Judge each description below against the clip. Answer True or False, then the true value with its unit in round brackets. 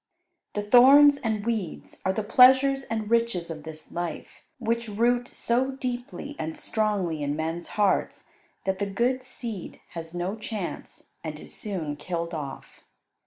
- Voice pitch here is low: False (210 Hz)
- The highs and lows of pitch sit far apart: True (6.2 semitones)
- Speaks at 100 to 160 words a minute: True (150 wpm)